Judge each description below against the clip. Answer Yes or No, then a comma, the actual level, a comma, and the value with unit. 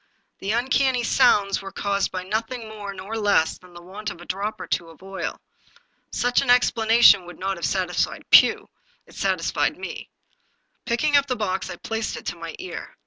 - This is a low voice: No, high, 200 Hz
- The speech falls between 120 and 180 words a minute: No, average, 195 wpm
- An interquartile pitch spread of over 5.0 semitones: No, average, 3.7 semitones